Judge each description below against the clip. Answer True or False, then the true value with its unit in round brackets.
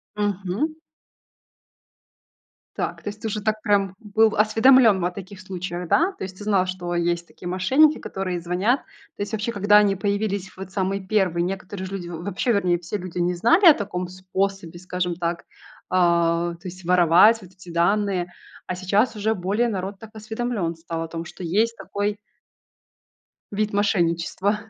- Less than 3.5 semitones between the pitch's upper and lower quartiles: True (2.9 semitones)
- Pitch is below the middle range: False (190 Hz)